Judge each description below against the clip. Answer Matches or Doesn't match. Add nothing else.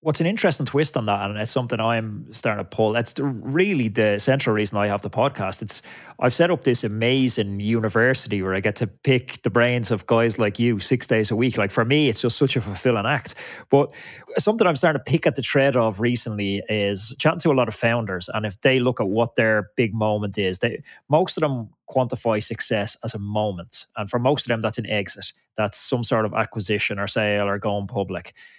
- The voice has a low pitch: Matches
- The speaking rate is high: Matches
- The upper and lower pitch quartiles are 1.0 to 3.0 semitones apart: Doesn't match